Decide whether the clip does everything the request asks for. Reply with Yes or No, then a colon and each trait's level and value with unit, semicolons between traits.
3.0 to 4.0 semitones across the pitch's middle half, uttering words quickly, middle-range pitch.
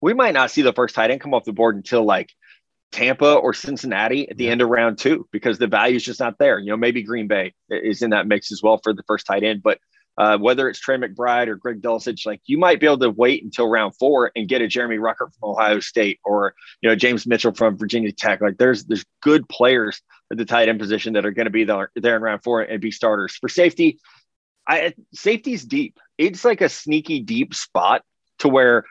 No: average, 3.7 semitones; fast, 245 wpm; low, 115 Hz